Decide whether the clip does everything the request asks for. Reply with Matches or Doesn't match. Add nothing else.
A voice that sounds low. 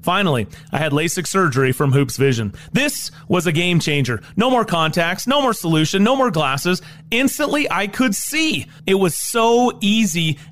Doesn't match